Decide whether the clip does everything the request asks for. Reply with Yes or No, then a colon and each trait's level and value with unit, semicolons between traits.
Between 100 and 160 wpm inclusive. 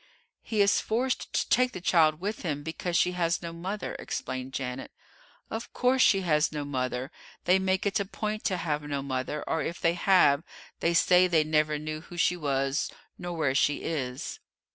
No: average, 190 wpm